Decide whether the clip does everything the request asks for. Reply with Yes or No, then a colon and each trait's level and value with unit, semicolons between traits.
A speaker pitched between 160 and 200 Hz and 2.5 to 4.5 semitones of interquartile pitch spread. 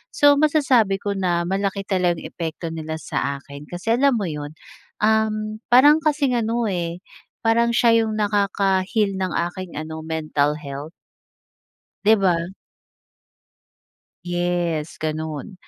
No: high, 190 Hz; wide, 5.4 semitones